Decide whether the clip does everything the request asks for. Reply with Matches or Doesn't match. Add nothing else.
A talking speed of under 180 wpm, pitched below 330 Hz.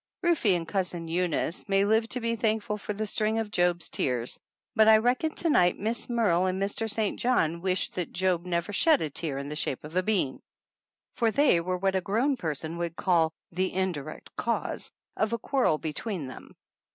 Doesn't match